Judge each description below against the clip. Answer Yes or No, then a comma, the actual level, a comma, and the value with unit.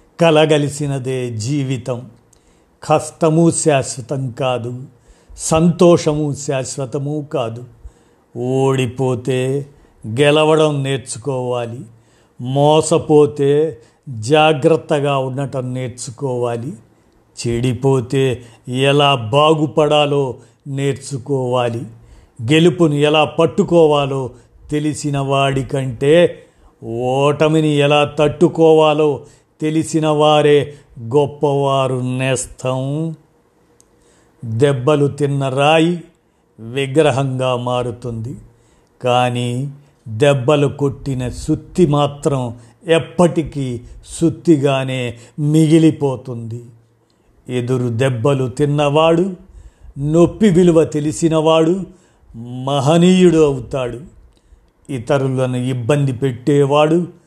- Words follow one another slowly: Yes, slow, 60 wpm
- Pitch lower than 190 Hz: Yes, medium, 140 Hz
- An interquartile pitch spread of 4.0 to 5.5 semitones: No, average, 3.4 semitones